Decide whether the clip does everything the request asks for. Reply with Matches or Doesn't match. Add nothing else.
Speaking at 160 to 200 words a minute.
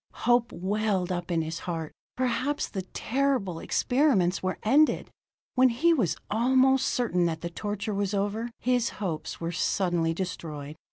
Doesn't match